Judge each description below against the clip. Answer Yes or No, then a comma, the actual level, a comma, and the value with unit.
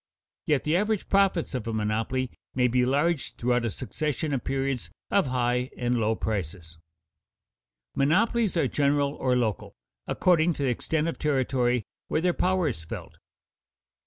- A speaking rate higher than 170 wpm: No, average, 155 wpm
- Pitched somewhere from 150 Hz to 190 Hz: No, low, 135 Hz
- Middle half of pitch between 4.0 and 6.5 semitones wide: Yes, average, 4.7 semitones